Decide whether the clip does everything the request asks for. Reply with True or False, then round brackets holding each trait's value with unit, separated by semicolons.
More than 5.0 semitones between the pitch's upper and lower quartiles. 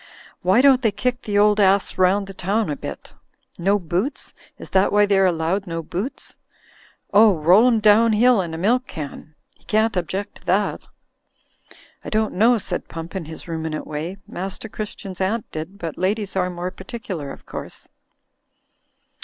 False (3.7 semitones)